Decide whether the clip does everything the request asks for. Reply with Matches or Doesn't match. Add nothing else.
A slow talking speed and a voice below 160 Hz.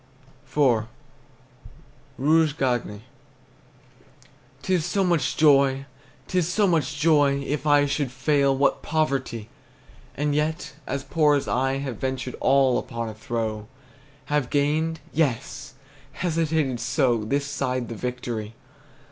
Matches